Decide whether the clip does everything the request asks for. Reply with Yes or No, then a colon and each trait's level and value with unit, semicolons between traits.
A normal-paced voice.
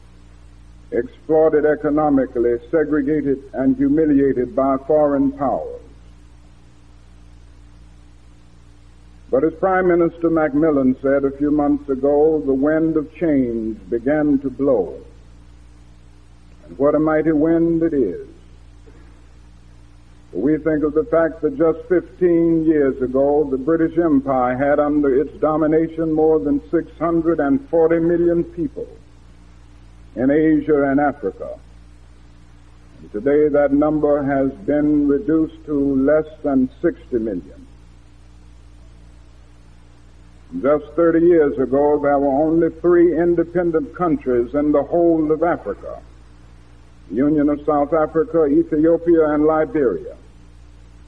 No: slow, 110 wpm